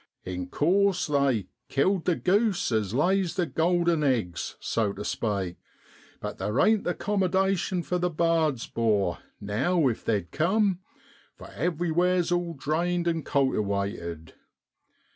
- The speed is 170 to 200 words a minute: No, slow, 135 wpm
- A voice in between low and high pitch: Yes, medium, 160 Hz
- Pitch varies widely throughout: Yes, wide, 8.3 semitones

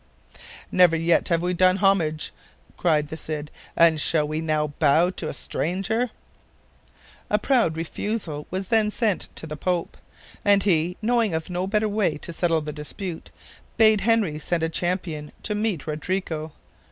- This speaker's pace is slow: No, average, 160 wpm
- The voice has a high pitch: No, medium, 175 Hz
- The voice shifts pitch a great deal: No, average, 4.2 semitones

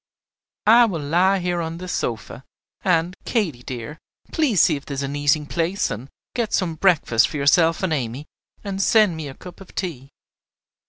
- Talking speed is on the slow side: No, average, 180 wpm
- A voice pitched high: No, medium, 165 Hz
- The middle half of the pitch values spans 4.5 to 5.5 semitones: Yes, average, 5.0 semitones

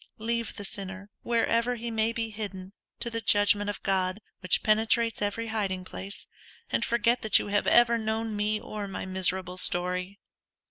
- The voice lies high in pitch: Yes, high, 210 Hz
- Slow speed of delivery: No, average, 170 wpm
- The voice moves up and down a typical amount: Yes, average, 3.0 semitones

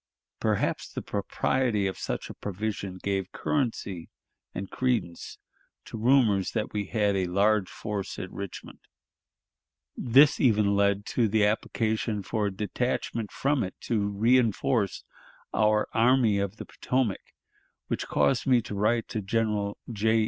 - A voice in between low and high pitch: No, low, 105 Hz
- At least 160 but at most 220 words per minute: No, slow, 135 wpm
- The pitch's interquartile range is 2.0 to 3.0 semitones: Yes, narrow, 2.6 semitones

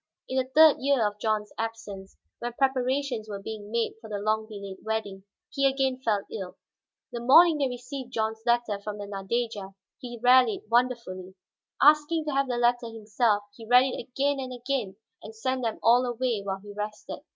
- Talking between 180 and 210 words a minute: Yes, average, 185 wpm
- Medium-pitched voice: No, high, 235 Hz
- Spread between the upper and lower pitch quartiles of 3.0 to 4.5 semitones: Yes, average, 3.5 semitones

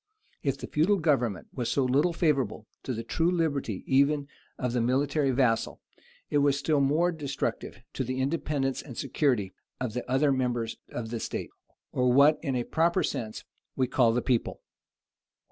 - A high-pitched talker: No, low, 135 Hz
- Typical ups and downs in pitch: Yes, average, 3.3 semitones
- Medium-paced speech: Yes, average, 170 wpm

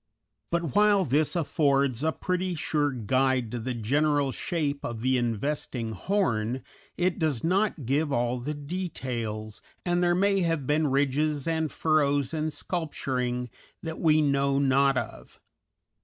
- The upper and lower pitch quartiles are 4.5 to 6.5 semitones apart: No, average, 4.0 semitones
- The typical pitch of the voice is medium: Yes, medium, 145 Hz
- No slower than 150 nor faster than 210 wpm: No, average, 140 wpm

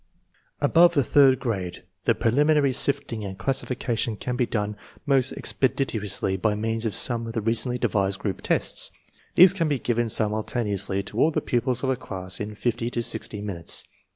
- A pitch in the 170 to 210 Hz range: No, low, 115 Hz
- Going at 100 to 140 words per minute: No, average, 180 wpm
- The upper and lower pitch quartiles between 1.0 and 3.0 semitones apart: No, average, 3.9 semitones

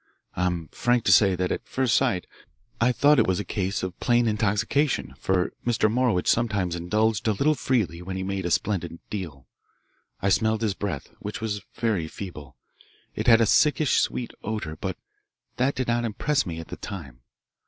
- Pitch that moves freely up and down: No, average, 4.5 semitones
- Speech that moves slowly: No, average, 185 wpm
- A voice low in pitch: Yes, low, 105 Hz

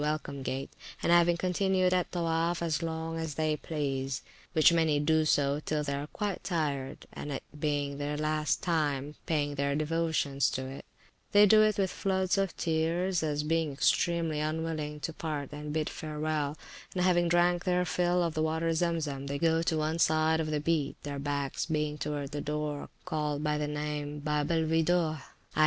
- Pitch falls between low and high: Yes, medium, 155 Hz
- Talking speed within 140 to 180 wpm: No, average, 190 wpm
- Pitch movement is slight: Yes, narrow, 2.2 semitones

